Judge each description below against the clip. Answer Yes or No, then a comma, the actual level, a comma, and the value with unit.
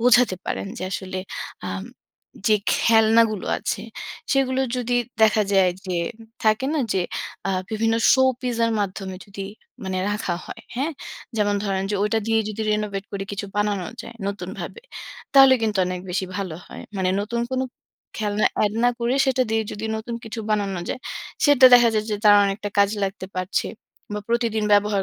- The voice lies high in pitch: Yes, high, 210 Hz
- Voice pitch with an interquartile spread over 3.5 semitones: No, average, 2.9 semitones